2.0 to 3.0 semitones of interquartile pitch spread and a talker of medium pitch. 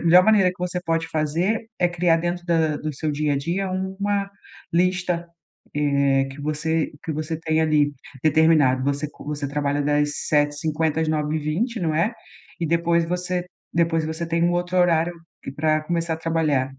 Yes: narrow, 2.6 semitones; medium, 160 Hz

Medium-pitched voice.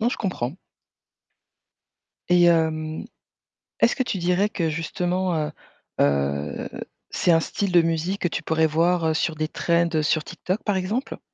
Yes: medium, 170 Hz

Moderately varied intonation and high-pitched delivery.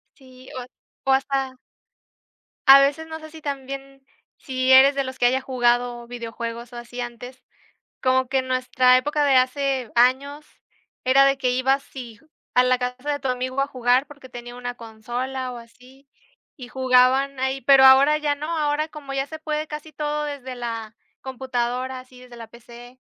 No: narrow, 1.9 semitones; very high, 260 Hz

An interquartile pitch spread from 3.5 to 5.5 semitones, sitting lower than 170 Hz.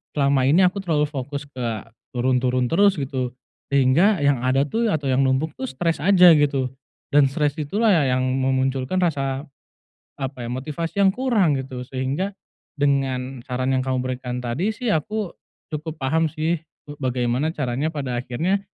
Yes: average, 4.1 semitones; medium, 140 Hz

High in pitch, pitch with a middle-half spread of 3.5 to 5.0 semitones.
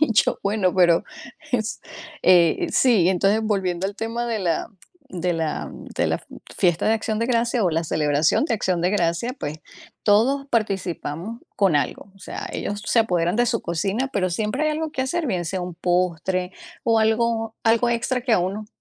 Yes: high, 205 Hz; average, 4.6 semitones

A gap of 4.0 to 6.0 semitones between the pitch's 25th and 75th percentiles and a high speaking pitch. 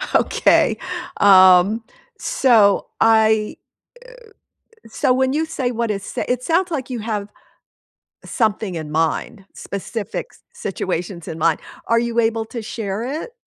No: average, 3.6 semitones; high, 220 Hz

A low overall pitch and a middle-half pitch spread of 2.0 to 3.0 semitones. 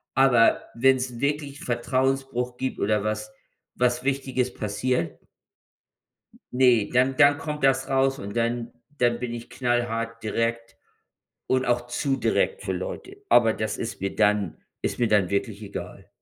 Yes: low, 120 Hz; average, 2.7 semitones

